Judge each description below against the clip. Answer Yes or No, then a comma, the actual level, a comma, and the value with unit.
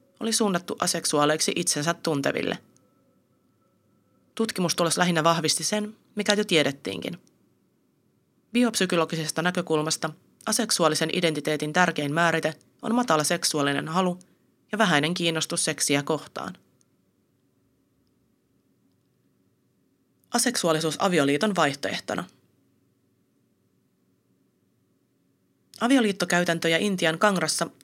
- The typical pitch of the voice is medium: Yes, medium, 165 Hz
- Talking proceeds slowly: Yes, slow, 75 wpm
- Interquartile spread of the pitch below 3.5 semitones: No, average, 4.2 semitones